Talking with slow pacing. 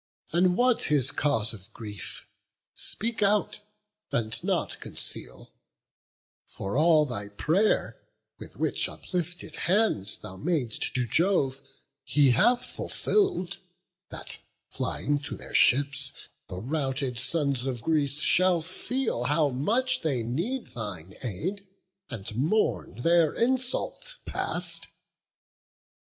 Yes: slow, 110 wpm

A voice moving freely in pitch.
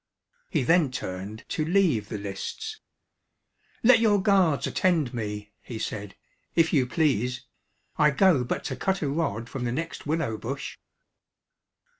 Yes: wide, 6.9 semitones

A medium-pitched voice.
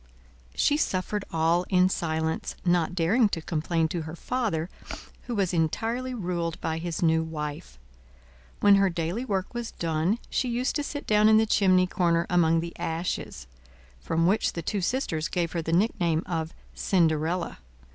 Yes: medium, 175 Hz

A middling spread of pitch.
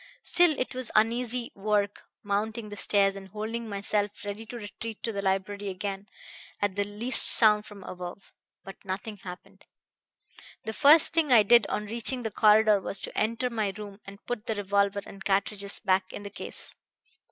No: narrow, 2.1 semitones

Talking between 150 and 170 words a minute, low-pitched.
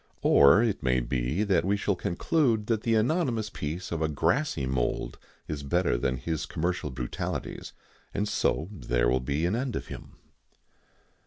Yes: average, 160 wpm; very low, 85 Hz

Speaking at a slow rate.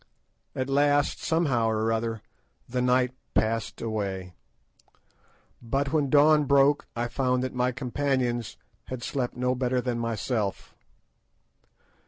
Yes: slow, 120 wpm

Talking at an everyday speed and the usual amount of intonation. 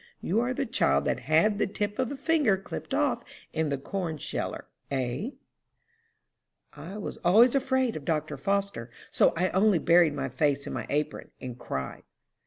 No: average, 175 wpm; wide, 7.2 semitones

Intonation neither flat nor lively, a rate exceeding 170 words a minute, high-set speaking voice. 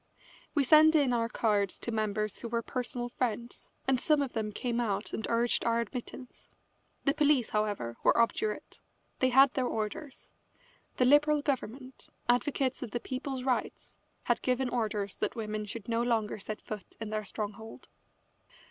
No: average, 3.4 semitones; average, 165 wpm; high, 240 Hz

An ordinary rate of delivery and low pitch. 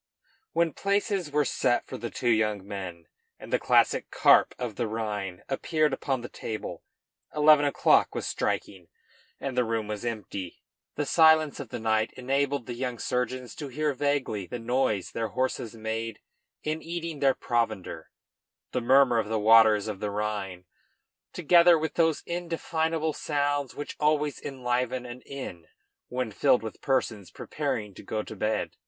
Yes: average, 160 wpm; low, 125 Hz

